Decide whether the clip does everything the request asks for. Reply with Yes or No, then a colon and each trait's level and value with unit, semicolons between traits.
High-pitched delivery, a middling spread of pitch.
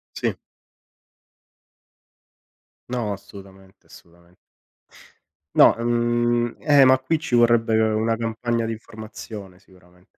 No: low, 115 Hz; average, 3.3 semitones